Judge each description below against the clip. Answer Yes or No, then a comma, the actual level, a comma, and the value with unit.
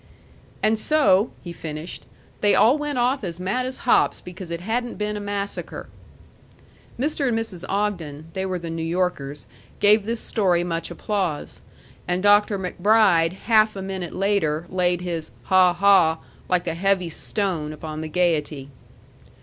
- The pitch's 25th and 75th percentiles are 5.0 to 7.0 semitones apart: No, average, 3.8 semitones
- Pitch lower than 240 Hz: Yes, medium, 185 Hz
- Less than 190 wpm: Yes, average, 155 wpm